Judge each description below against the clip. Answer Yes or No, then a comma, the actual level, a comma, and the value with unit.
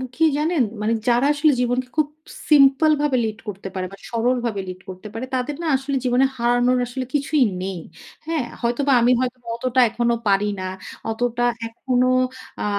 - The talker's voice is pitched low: No, high, 245 Hz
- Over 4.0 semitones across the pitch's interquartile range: No, average, 2.8 semitones